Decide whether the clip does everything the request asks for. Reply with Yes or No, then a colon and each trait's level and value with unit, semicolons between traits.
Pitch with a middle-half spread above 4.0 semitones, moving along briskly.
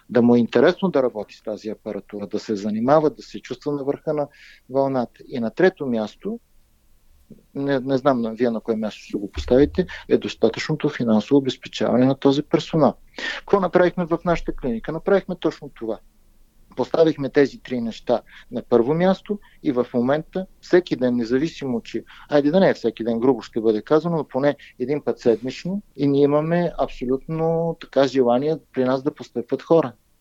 Yes: wide, 5.6 semitones; fast, 175 wpm